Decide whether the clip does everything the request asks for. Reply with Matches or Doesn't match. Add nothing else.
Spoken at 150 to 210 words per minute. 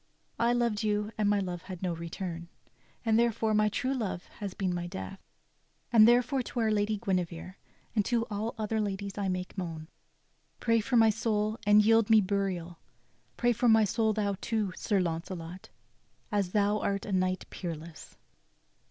Matches